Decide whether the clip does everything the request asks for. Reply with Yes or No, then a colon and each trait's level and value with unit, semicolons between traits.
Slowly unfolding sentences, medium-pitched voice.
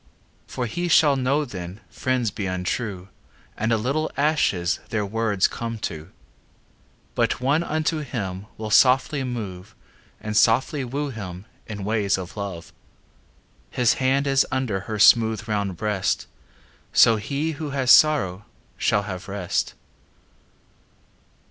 No: slow, 130 wpm; low, 110 Hz